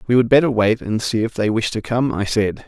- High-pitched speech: No, low, 115 Hz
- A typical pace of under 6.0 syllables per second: Yes, 5.6 syllables/s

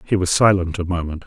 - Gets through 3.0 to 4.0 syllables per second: No, 6.2 syllables/s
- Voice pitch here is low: Yes, very low, 90 Hz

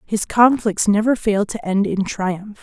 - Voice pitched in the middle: No, high, 205 Hz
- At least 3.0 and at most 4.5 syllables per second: Yes, 4.0 syllables/s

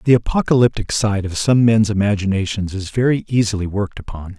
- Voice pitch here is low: Yes, low, 105 Hz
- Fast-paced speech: No, average, 165 wpm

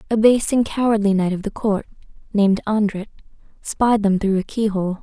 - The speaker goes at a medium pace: Yes, average, 180 wpm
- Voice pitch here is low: No, high, 205 Hz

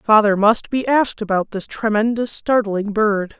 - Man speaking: No, female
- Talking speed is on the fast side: No, average, 160 wpm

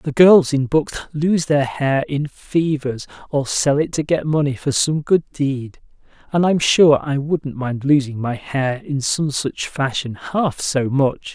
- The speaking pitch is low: No, medium, 145 Hz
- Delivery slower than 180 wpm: No, average, 185 wpm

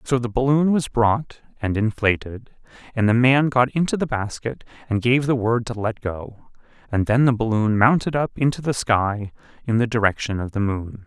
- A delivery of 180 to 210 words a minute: Yes, average, 195 wpm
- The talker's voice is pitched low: Yes, low, 120 Hz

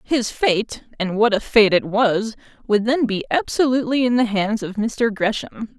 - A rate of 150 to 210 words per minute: Yes, average, 165 wpm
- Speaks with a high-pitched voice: Yes, high, 225 Hz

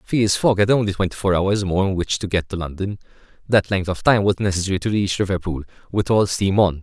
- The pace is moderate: No, fast, 235 wpm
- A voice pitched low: Yes, very low, 95 Hz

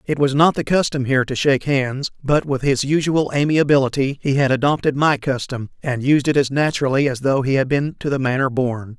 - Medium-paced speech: No, fast, 220 wpm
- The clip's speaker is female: No, male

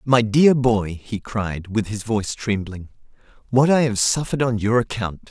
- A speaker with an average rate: Yes, average, 180 wpm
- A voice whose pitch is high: No, low, 110 Hz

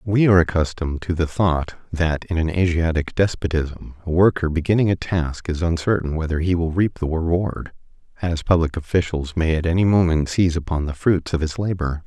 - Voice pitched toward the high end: No, very low, 85 Hz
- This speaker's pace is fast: No, average, 190 wpm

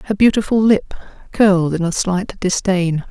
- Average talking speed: Yes, average, 155 wpm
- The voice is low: No, high, 190 Hz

